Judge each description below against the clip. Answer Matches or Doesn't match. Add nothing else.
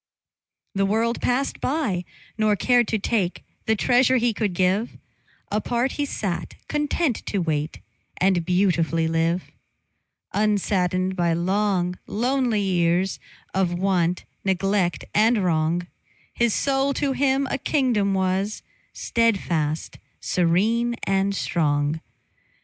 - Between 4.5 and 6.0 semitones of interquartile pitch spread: Matches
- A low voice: Doesn't match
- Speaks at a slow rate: Matches